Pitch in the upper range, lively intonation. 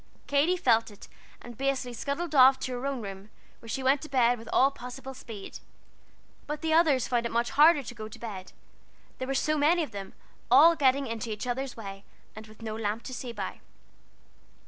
No: very high, 250 Hz; average, 3.7 semitones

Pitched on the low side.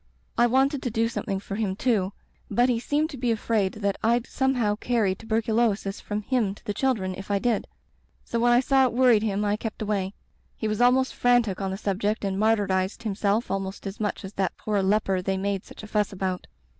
No: high, 215 Hz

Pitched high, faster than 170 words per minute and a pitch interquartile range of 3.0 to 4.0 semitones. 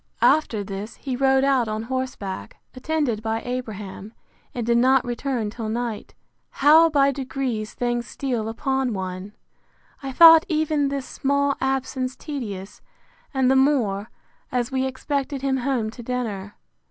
No: very high, 255 Hz; average, 140 wpm; average, 3.6 semitones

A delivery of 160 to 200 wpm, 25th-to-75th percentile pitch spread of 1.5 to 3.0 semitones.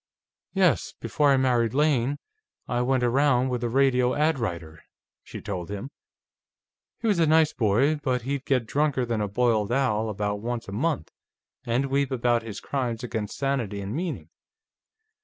No: average, 165 wpm; average, 3.7 semitones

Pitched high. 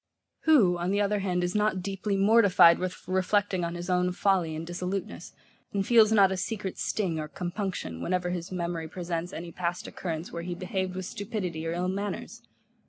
No: medium, 180 Hz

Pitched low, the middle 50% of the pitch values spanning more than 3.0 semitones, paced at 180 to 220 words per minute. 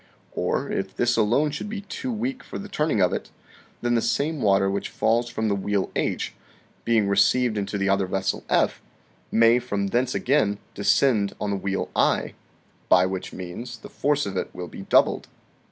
Yes: low, 110 Hz; average, 4.2 semitones; average, 190 wpm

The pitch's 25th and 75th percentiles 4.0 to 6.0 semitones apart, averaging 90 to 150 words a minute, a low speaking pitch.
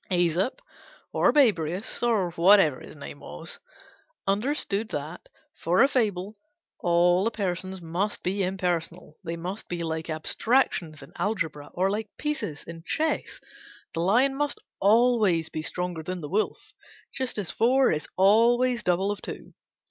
No: average, 4.8 semitones; average, 145 wpm; high, 190 Hz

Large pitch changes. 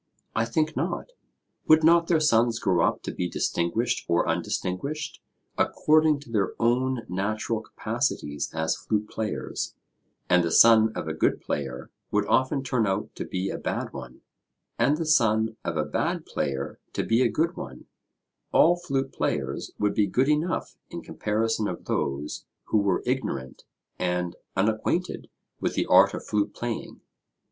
Yes: wide, 6.5 semitones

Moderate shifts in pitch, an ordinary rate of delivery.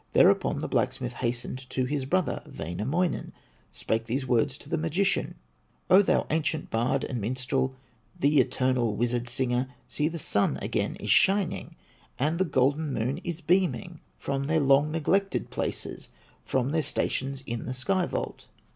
Yes: average, 4.3 semitones; average, 155 wpm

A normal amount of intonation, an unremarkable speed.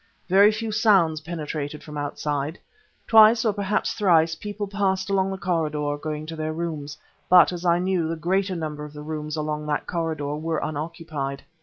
Yes: average, 3.9 semitones; average, 175 wpm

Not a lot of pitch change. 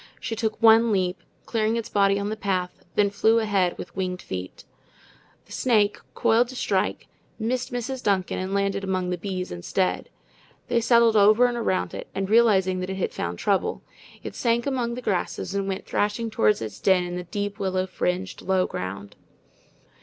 No: average, 3.6 semitones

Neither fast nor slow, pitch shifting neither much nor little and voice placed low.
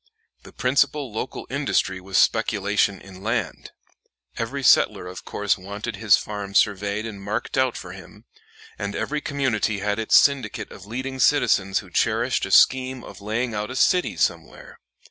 Yes: average, 160 wpm; average, 4.4 semitones; low, 105 Hz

